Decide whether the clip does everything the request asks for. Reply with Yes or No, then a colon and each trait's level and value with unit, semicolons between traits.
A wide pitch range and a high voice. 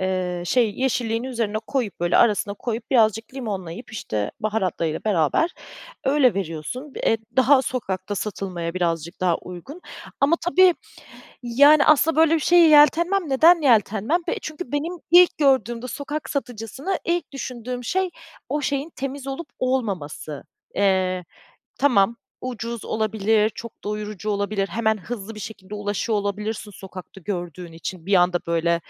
Yes: wide, 6.1 semitones; high, 220 Hz